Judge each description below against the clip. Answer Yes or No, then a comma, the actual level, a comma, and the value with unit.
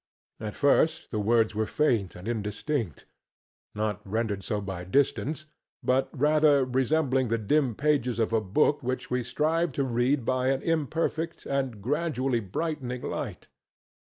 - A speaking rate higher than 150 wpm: No, average, 140 wpm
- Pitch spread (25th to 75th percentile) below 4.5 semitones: No, average, 5.1 semitones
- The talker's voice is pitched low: Yes, low, 125 Hz